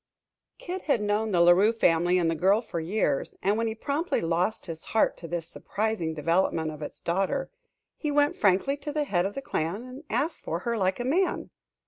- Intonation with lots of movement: Yes, wide, 6.6 semitones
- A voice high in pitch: Yes, high, 200 Hz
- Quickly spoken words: Yes, fast, 210 wpm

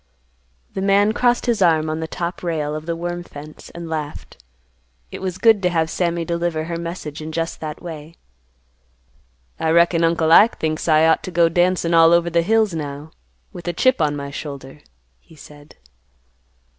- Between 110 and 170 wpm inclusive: No, average, 185 wpm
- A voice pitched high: No, medium, 165 Hz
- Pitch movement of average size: No, narrow, 2.1 semitones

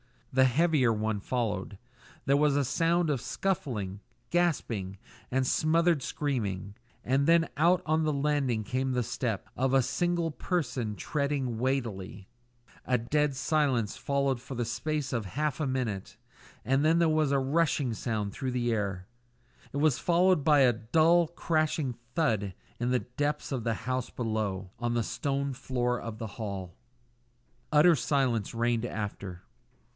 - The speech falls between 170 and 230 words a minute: No, average, 155 wpm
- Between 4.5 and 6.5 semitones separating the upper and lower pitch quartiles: Yes, average, 4.8 semitones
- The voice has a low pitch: Yes, low, 130 Hz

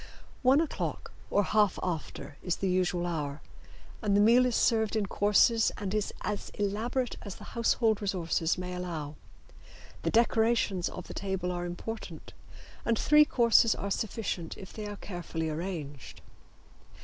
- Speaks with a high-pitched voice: Yes, high, 200 Hz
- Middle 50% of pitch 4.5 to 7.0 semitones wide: No, average, 4.1 semitones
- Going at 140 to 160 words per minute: Yes, average, 150 wpm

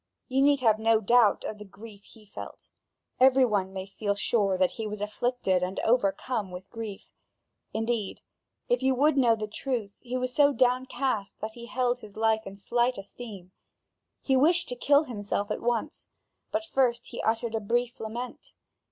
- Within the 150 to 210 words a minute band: Yes, average, 180 wpm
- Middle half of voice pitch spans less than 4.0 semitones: Yes, average, 3.6 semitones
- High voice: Yes, high, 225 Hz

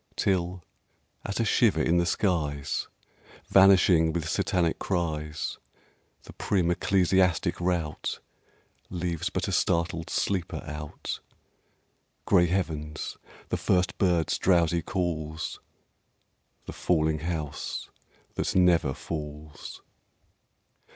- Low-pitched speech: Yes, very low, 85 Hz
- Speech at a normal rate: No, slow, 95 wpm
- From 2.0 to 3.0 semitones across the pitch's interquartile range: Yes, average, 2.7 semitones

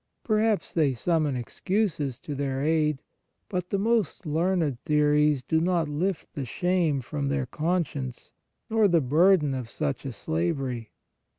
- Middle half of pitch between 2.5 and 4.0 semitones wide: No, average, 4.7 semitones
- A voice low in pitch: No, medium, 150 Hz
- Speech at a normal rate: Yes, average, 150 wpm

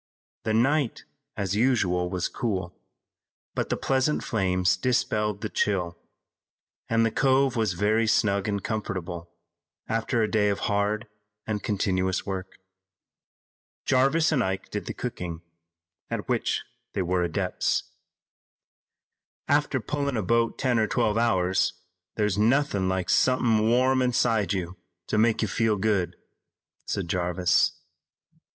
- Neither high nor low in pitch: No, low, 105 Hz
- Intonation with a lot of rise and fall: No, average, 4.0 semitones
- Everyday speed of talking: No, slow, 130 wpm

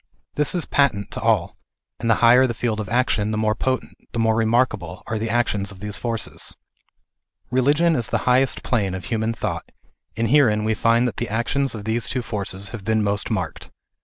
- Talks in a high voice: No, low, 115 Hz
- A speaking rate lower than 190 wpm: No, average, 200 wpm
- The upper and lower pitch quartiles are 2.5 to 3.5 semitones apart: Yes, average, 2.8 semitones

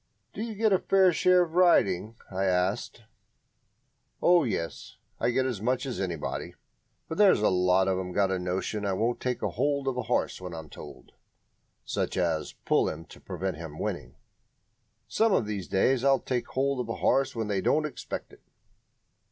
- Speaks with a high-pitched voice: No, low, 110 Hz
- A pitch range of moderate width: No, wide, 7.0 semitones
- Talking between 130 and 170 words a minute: No, average, 185 wpm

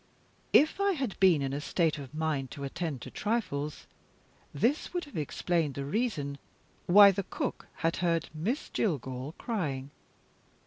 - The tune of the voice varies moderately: No, wide, 6.5 semitones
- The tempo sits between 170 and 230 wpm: No, average, 150 wpm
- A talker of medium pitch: Yes, medium, 165 Hz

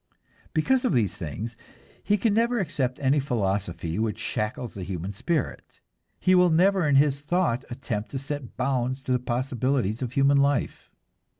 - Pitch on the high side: No, low, 130 Hz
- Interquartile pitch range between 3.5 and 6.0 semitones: Yes, average, 4.9 semitones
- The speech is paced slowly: No, average, 165 wpm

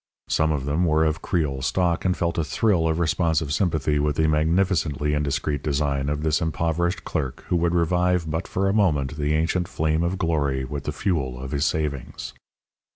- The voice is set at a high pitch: No, very low, 80 Hz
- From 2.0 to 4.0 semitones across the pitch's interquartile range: Yes, average, 2.8 semitones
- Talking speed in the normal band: Yes, average, 190 wpm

